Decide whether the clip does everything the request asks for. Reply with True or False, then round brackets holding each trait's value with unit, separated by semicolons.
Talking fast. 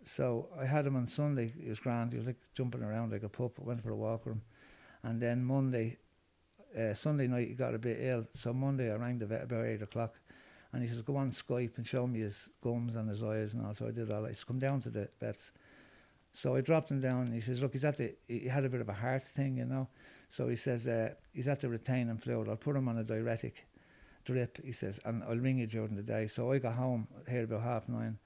True (270 wpm)